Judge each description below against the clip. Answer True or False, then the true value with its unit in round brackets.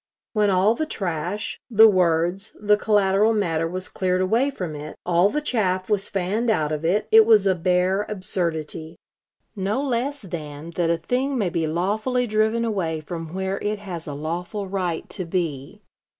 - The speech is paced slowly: False (175 wpm)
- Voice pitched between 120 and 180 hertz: False (190 Hz)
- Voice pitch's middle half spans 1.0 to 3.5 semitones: False (4.0 semitones)